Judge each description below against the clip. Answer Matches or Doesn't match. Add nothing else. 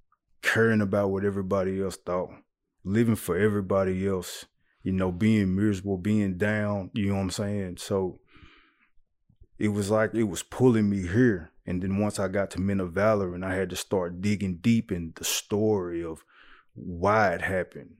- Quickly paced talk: Doesn't match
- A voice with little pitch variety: Matches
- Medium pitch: Doesn't match